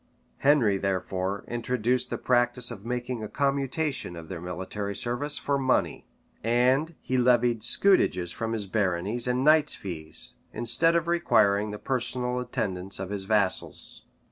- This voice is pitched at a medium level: No, low, 120 Hz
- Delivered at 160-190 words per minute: No, average, 140 wpm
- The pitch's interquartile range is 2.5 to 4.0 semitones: No, average, 4.4 semitones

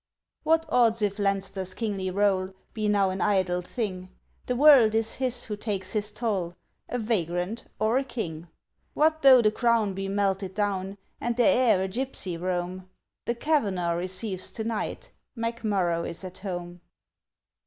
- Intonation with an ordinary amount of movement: Yes, average, 3.7 semitones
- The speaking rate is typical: Yes, average, 155 wpm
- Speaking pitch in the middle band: No, high, 205 Hz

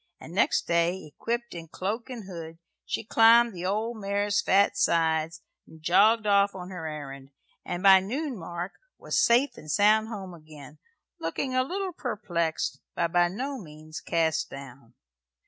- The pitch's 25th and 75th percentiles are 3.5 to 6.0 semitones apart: Yes, average, 5.2 semitones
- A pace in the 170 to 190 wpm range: No, average, 160 wpm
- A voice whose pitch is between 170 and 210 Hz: Yes, high, 190 Hz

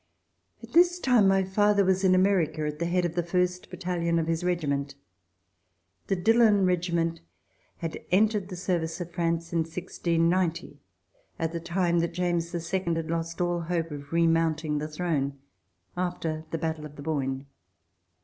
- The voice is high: No, medium, 170 Hz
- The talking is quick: No, average, 165 wpm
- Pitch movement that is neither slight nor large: No, narrow, 2.0 semitones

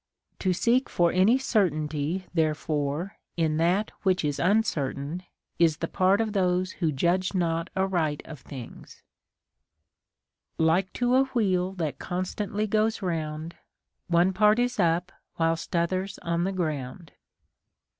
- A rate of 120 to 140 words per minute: Yes, slow, 135 wpm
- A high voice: No, medium, 180 Hz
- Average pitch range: Yes, average, 3.3 semitones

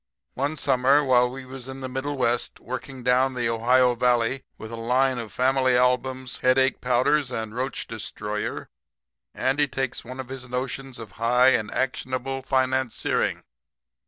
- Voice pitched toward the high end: No, low, 130 Hz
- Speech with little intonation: Yes, narrow, 1.3 semitones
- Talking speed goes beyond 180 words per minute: No, average, 155 wpm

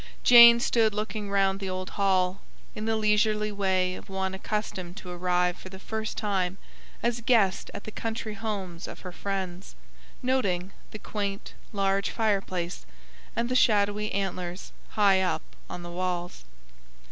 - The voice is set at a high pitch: Yes, high, 195 Hz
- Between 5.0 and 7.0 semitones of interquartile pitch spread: No, narrow, 2.6 semitones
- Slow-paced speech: No, average, 150 wpm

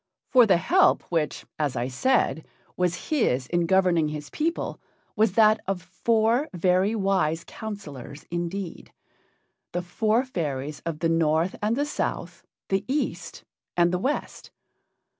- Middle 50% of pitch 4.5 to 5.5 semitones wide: Yes, average, 5.1 semitones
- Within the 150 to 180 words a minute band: No, average, 140 wpm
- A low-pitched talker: No, medium, 180 Hz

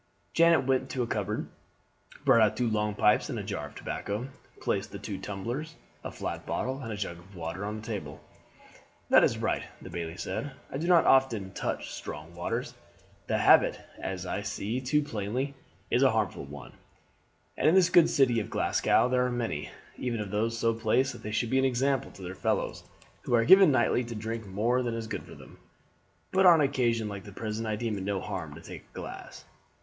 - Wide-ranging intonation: No, average, 4.3 semitones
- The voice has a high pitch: No, low, 115 Hz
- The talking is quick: Yes, fast, 210 wpm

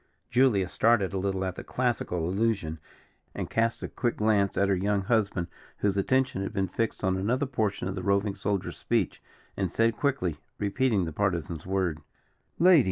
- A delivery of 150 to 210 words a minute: Yes, average, 175 wpm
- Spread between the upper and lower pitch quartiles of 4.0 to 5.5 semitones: No, average, 3.4 semitones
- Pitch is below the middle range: Yes, low, 100 Hz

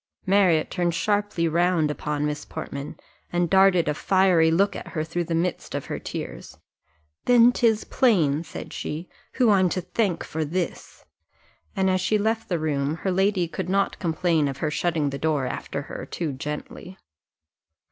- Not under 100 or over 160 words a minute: No, average, 170 wpm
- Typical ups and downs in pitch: Yes, average, 3.7 semitones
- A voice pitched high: No, medium, 175 Hz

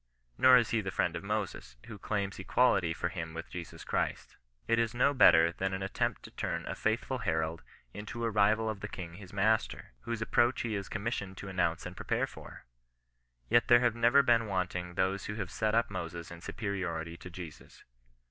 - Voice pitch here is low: Yes, low, 100 Hz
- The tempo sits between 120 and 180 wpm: No, fast, 205 wpm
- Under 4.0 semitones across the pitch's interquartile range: No, average, 4.4 semitones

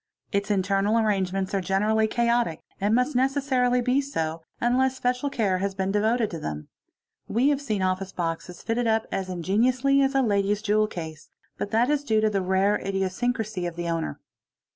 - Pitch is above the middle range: Yes, high, 210 Hz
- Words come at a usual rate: Yes, average, 180 wpm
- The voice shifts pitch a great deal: No, average, 4.5 semitones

